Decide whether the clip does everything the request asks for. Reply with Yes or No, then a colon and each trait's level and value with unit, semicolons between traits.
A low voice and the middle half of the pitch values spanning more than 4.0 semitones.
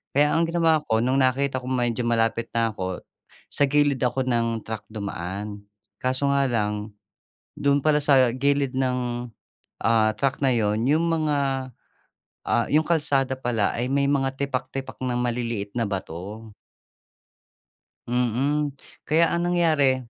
No: low, 130 Hz; average, 3.6 semitones